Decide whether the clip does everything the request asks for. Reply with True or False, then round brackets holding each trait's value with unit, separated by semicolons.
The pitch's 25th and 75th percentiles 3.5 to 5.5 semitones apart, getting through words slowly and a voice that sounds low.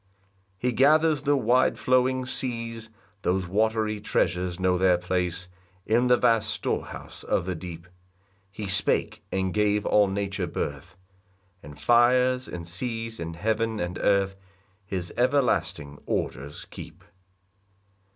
True (5.1 semitones; 130 wpm; 105 Hz)